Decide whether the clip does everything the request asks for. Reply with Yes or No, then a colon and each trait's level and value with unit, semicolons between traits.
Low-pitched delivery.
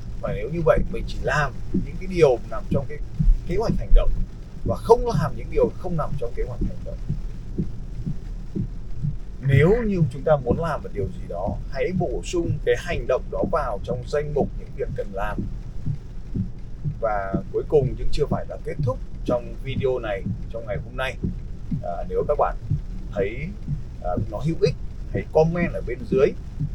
No: medium, 150 Hz